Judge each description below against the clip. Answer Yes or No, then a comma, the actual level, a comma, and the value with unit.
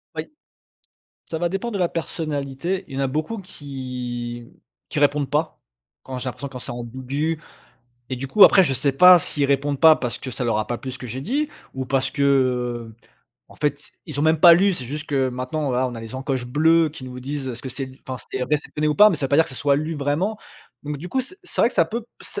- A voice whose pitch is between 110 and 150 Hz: Yes, medium, 140 Hz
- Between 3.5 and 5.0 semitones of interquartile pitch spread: Yes, average, 3.8 semitones